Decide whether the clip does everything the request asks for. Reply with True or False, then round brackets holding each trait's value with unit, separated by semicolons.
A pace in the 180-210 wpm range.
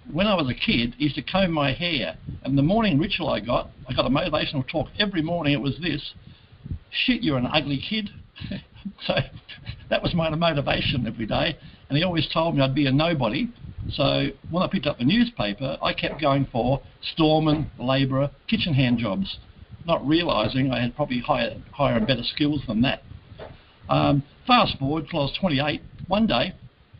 True (190 wpm)